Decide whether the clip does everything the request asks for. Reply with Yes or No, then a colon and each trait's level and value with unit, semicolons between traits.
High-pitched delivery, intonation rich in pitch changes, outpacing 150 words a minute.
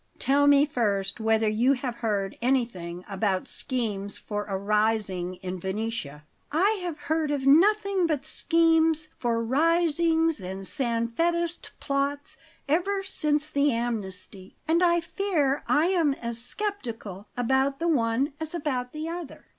No: very high, 270 Hz; wide, 6.7 semitones; average, 140 wpm